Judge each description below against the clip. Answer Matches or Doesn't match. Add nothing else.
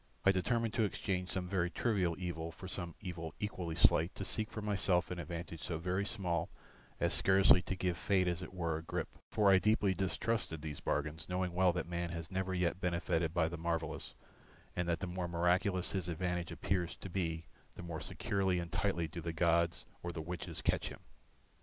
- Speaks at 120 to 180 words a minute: Doesn't match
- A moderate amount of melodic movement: Doesn't match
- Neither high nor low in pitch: Doesn't match